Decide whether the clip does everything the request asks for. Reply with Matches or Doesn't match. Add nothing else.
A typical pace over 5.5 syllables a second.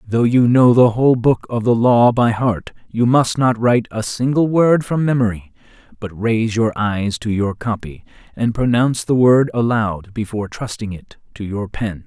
Doesn't match